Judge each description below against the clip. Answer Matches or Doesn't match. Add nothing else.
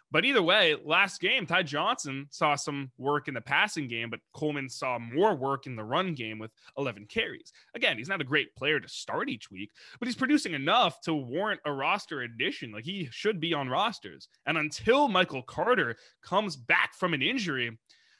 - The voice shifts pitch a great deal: Matches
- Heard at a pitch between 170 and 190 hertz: Doesn't match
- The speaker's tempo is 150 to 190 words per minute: Doesn't match